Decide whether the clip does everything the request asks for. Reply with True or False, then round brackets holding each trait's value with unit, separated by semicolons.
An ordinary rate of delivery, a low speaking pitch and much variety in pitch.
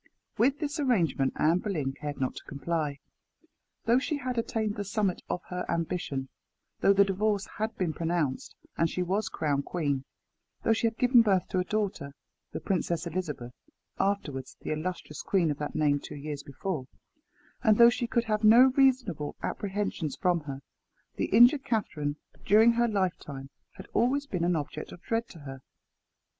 False (170 wpm; 185 Hz; 6.9 semitones)